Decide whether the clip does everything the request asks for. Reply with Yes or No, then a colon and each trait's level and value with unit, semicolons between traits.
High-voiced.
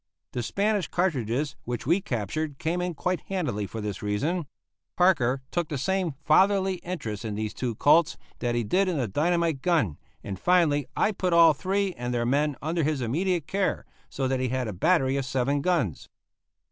No: medium, 150 Hz